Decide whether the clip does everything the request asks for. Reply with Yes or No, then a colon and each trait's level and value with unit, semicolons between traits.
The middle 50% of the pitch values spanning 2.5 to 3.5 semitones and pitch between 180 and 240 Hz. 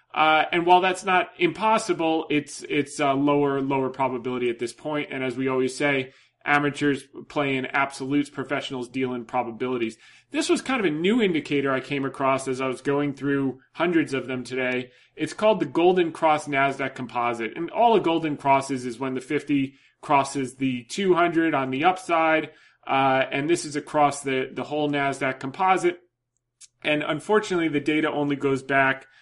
No: average, 3.1 semitones; medium, 140 Hz